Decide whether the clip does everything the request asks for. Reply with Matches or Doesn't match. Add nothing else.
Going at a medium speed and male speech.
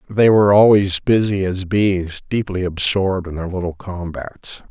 Matches